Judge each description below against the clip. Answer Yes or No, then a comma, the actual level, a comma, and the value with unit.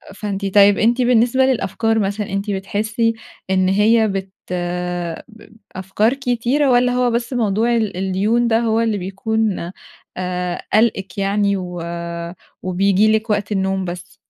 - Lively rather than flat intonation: No, average, 3.1 semitones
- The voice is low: No, high, 210 Hz